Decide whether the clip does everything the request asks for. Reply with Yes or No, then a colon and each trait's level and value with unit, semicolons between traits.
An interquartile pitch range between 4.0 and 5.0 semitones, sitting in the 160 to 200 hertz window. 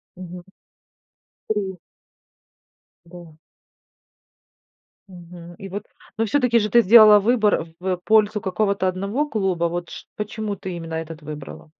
No: average, 3.6 semitones; high, 190 Hz